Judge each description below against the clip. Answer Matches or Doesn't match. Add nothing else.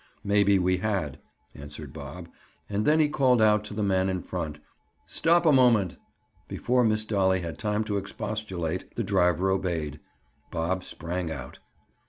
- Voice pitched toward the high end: Doesn't match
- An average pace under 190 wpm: Matches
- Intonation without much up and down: Doesn't match